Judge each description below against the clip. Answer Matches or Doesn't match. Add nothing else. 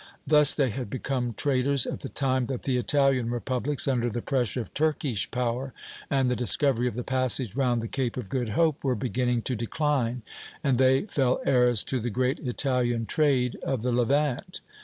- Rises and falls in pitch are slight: Matches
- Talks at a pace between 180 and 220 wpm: Matches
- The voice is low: Matches